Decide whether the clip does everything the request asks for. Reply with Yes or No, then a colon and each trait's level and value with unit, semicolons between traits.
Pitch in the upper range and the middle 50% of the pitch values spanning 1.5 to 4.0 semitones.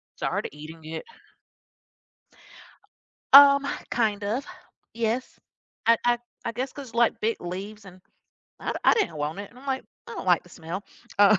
No: high, 215 Hz; average, 5.3 semitones